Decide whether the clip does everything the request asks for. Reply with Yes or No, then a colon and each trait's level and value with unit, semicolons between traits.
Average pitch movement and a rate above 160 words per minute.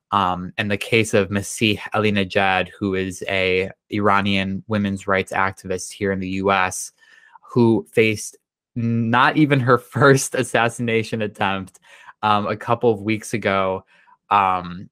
No: average, 3.2 semitones; slow, 135 wpm